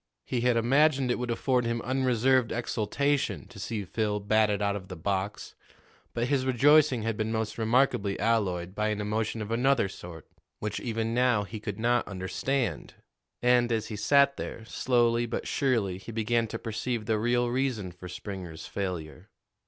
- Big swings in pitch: No, average, 3.2 semitones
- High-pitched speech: No, low, 115 Hz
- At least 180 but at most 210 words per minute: No, average, 170 wpm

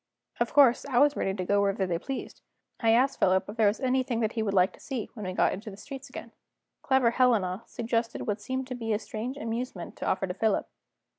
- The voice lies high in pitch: Yes, high, 225 Hz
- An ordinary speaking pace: No, fast, 230 wpm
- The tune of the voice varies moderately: Yes, average, 4.1 semitones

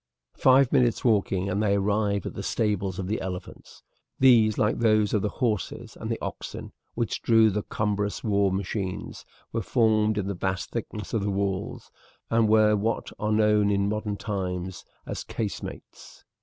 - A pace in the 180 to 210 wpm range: No, average, 170 wpm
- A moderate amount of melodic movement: No, narrow, 1.8 semitones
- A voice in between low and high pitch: No, low, 105 Hz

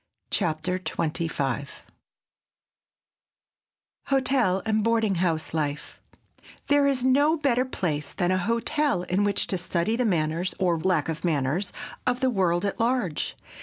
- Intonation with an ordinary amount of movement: No, wide, 6.6 semitones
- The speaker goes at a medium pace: No, slow, 130 wpm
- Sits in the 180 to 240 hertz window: Yes, medium, 185 Hz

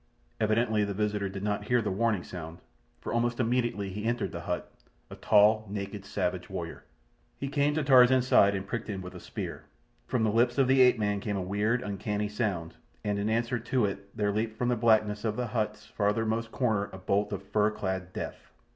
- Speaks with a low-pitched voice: Yes, low, 105 Hz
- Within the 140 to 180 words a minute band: No, fast, 205 wpm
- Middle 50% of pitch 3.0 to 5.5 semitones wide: No, narrow, 2.6 semitones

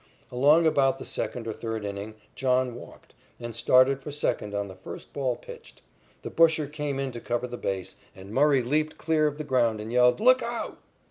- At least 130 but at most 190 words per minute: No, average, 200 wpm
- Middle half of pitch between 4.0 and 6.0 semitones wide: Yes, average, 4.4 semitones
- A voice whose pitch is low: Yes, low, 130 Hz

